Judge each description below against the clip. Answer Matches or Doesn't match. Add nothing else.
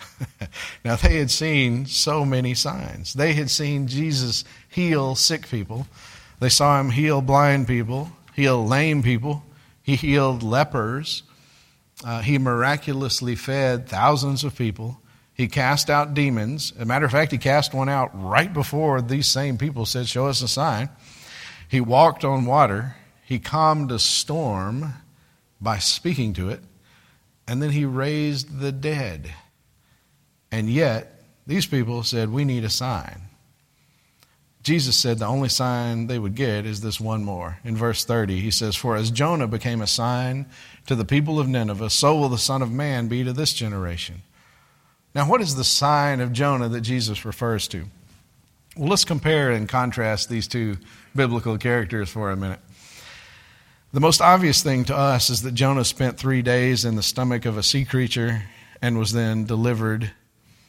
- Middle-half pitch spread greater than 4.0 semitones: Doesn't match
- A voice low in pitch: Matches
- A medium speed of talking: Matches